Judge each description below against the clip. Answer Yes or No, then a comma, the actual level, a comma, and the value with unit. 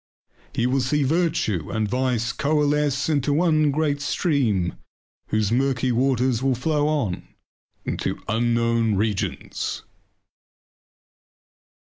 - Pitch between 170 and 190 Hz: No, low, 130 Hz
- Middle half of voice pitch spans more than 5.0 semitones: No, average, 4.1 semitones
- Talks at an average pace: No, slow, 100 wpm